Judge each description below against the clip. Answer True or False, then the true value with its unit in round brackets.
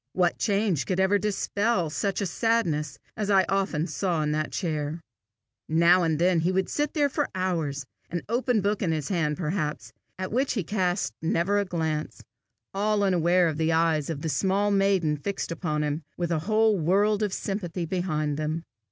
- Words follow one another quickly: False (185 wpm)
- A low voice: False (180 Hz)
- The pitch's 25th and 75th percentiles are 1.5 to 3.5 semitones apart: False (4.1 semitones)